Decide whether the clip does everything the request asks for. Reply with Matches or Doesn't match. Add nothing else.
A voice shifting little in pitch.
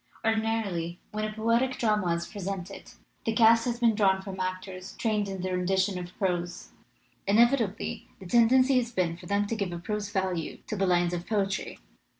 Doesn't match